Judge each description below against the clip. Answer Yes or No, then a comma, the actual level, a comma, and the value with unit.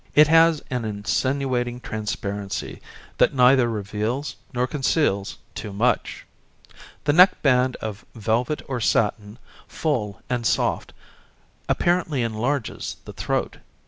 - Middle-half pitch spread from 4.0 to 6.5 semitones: Yes, average, 4.4 semitones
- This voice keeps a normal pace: No, slow, 110 wpm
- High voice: No, low, 125 Hz